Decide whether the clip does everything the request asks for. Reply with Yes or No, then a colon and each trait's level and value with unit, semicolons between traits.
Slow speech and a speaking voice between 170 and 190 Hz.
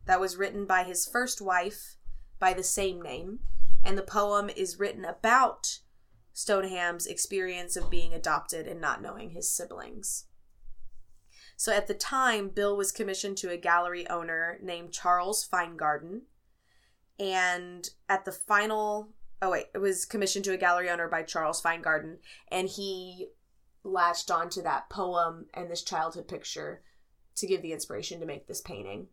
No: average, 155 wpm; medium, 185 Hz